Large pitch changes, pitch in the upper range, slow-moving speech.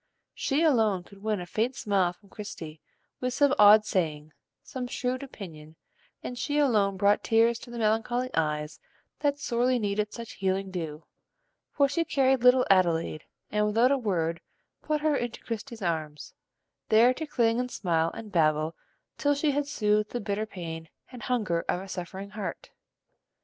No: wide, 5.8 semitones; high, 210 Hz; average, 165 wpm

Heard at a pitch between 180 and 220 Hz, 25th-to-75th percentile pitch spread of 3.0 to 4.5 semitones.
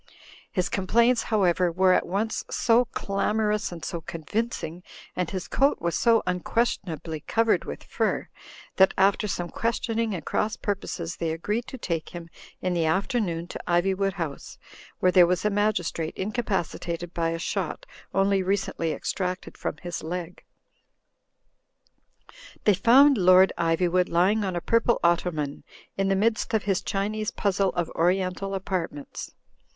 Yes: medium, 185 Hz; average, 3.5 semitones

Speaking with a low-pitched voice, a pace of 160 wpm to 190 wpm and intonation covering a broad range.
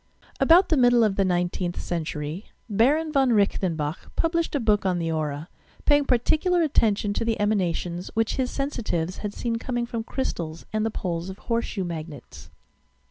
No: high, 210 Hz; average, 170 wpm; wide, 6.0 semitones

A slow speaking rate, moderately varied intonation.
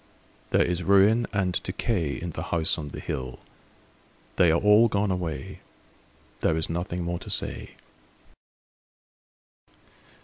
Yes: slow, 130 wpm; average, 3.5 semitones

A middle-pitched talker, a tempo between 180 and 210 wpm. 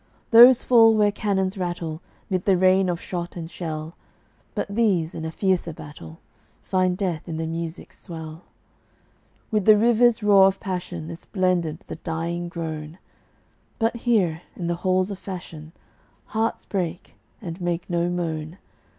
No: medium, 180 Hz; average, 150 wpm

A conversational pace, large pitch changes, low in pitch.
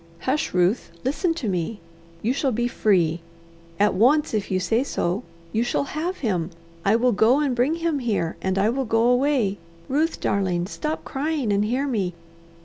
No: average, 180 wpm; wide, 6.0 semitones; high, 235 Hz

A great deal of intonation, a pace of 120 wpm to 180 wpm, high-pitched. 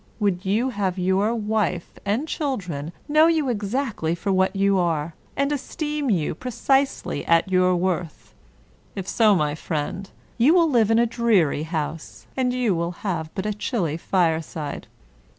Yes: wide, 5.9 semitones; average, 160 wpm; high, 195 Hz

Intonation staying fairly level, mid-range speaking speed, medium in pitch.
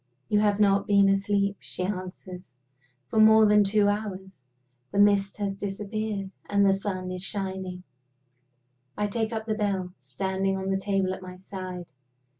No: narrow, 1.6 semitones; average, 160 wpm; high, 195 Hz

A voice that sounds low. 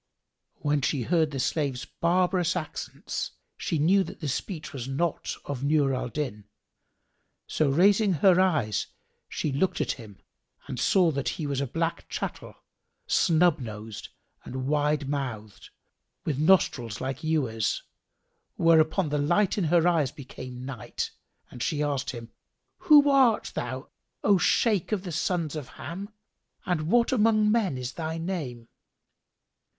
No: medium, 155 Hz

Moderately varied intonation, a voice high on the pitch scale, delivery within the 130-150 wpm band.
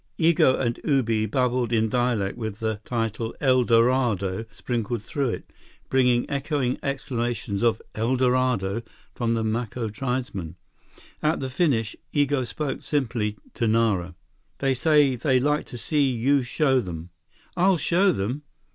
No: average, 3.3 semitones; low, 125 Hz; average, 140 wpm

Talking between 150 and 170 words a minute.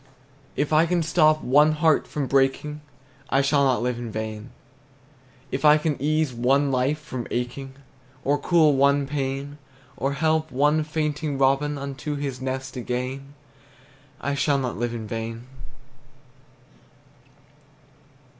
No: slow, 135 wpm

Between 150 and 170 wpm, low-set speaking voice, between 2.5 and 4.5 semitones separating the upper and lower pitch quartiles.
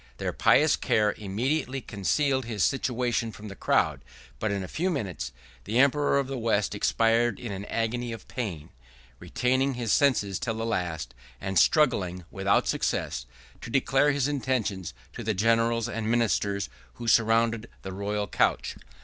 Yes: average, 160 wpm; low, 115 Hz; average, 3.9 semitones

